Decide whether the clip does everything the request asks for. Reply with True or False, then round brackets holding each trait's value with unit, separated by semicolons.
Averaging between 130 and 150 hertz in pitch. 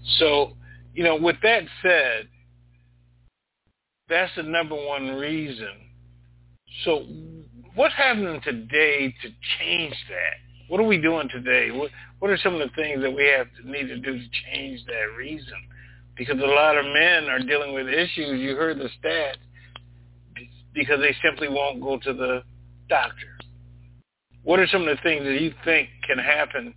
True (135 Hz)